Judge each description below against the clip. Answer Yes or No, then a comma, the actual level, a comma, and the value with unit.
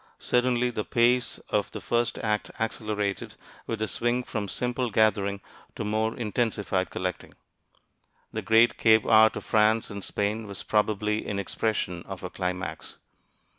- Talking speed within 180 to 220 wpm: No, average, 145 wpm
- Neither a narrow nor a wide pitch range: No, narrow, 2.2 semitones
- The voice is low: Yes, low, 110 Hz